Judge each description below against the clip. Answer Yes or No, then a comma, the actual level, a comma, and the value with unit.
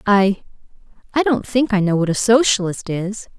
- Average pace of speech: Yes, average, 160 wpm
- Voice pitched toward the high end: Yes, high, 210 Hz